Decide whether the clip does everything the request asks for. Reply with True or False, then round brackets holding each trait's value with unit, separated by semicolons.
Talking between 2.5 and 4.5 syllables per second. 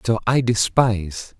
True (4.3 syllables/s)